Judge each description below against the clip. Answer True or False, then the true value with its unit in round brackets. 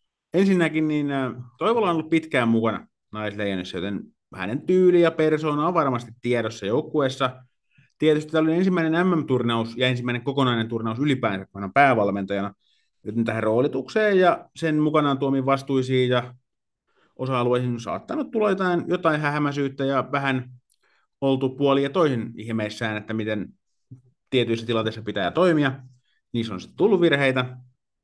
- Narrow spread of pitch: False (5.1 semitones)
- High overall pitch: False (130 Hz)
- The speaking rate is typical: True (130 wpm)